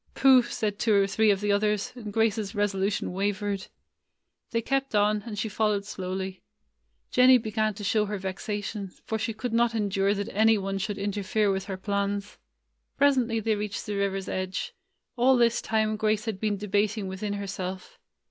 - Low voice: No, high, 205 Hz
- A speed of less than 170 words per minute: No, average, 175 wpm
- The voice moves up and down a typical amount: No, narrow, 1.9 semitones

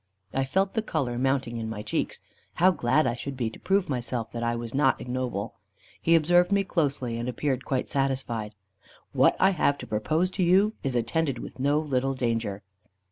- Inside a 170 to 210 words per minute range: Yes, average, 195 wpm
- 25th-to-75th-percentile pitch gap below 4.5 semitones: No, average, 5.2 semitones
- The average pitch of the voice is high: No, low, 135 Hz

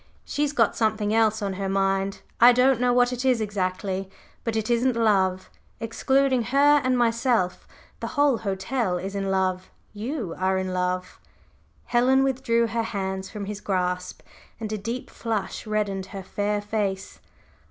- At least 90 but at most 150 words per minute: No, average, 160 wpm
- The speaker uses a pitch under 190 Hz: No, high, 215 Hz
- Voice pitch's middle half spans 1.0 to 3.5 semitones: No, average, 4.1 semitones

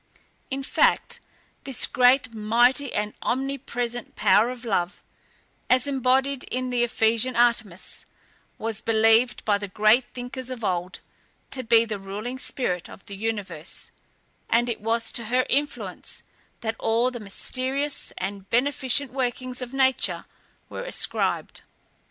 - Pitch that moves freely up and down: No, average, 2.9 semitones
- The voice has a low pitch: No, high, 240 Hz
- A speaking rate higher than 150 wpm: No, slow, 135 wpm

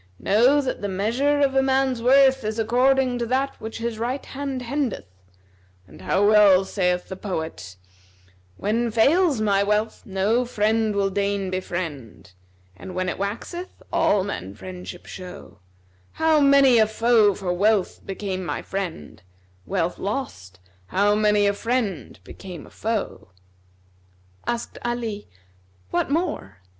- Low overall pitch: No, high, 210 Hz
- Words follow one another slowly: No, average, 145 wpm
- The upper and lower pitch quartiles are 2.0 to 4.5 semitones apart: No, average, 4.9 semitones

